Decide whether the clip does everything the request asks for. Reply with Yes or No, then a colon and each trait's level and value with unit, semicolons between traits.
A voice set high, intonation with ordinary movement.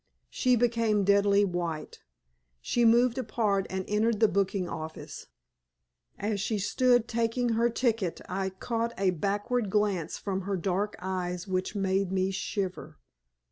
Yes: high, 200 Hz; average, 3.3 semitones